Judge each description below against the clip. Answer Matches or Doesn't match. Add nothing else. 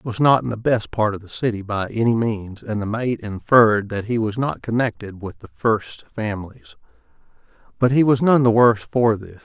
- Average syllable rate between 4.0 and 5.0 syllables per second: Doesn't match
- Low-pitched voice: Matches